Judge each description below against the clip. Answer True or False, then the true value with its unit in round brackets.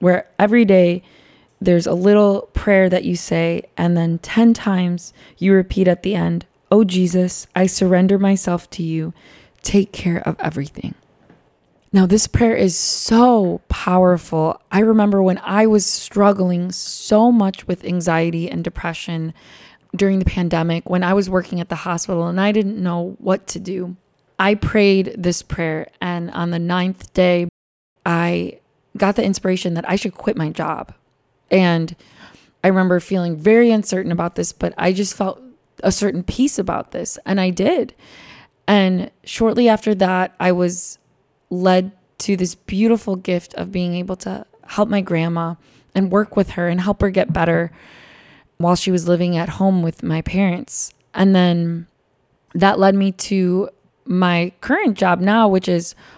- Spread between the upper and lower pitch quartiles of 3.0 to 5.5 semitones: False (2.4 semitones)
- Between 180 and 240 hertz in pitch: True (185 Hz)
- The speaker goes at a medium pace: True (160 wpm)